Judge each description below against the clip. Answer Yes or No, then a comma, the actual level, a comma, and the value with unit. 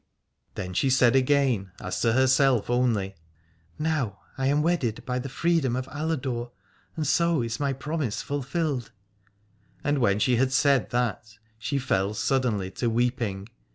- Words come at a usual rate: Yes, average, 150 wpm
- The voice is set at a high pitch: No, low, 125 Hz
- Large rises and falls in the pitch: No, average, 3.7 semitones